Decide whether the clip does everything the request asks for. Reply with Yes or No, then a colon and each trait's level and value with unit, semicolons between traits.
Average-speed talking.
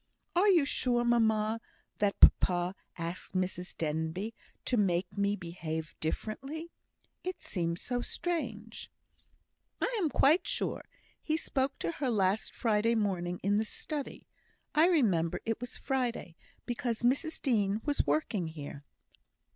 No: slow, 130 wpm